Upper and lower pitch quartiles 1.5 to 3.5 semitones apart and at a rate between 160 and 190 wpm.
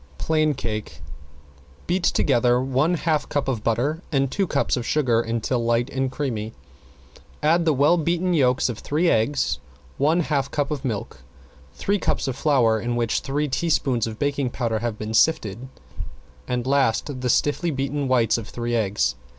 No: average, 4.2 semitones; average, 165 wpm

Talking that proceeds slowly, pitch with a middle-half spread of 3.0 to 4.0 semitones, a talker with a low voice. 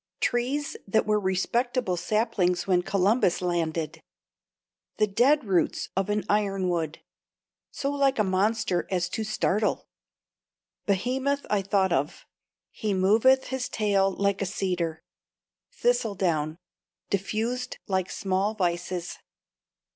No: slow, 115 wpm; average, 3.7 semitones; high, 200 Hz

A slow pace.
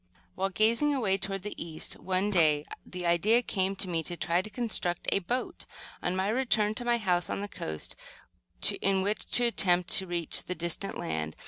No: average, 195 wpm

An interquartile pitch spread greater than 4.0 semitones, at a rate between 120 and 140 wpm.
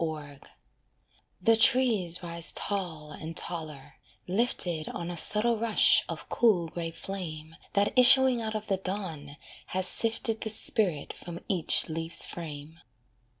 Yes: average, 5.1 semitones; slow, 135 wpm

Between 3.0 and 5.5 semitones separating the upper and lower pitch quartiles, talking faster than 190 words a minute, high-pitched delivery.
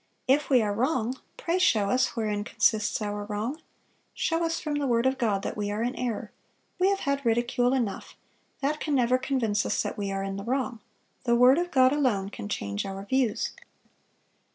Yes: average, 4.6 semitones; average, 200 wpm; high, 240 Hz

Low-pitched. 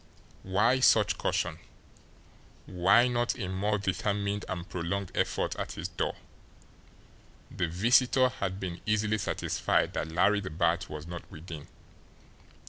Yes: very low, 95 Hz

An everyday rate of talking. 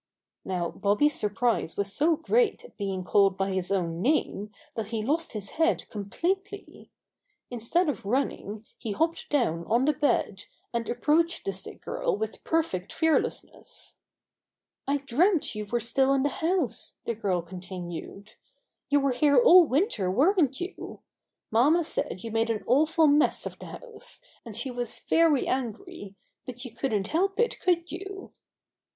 Yes: average, 160 wpm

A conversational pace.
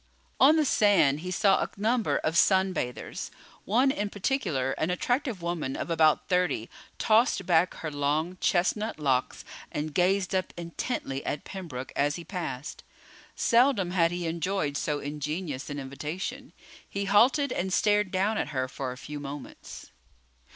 Yes: average, 155 wpm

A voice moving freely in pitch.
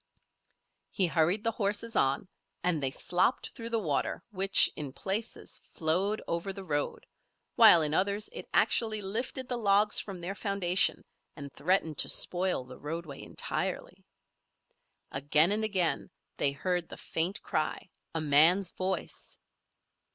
No: average, 4.3 semitones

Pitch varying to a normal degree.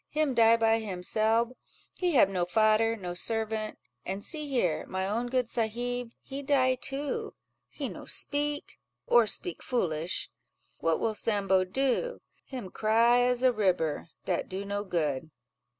Yes: average, 4.7 semitones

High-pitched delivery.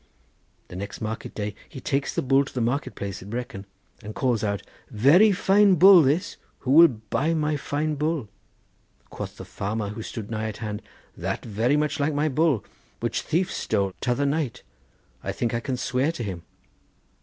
No: low, 130 Hz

